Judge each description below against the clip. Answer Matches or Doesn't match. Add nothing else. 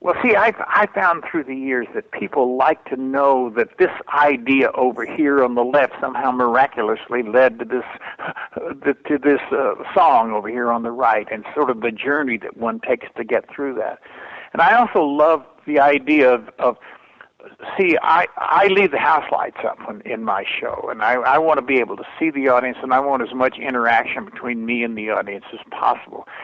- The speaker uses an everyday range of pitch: Matches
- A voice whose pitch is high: Doesn't match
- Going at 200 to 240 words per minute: Matches